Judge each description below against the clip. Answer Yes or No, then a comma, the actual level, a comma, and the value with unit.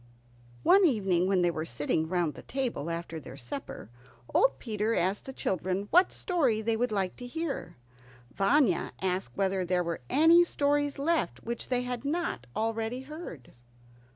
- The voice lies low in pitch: No, high, 220 Hz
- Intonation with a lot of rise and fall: Yes, wide, 7.6 semitones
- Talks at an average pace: Yes, average, 160 wpm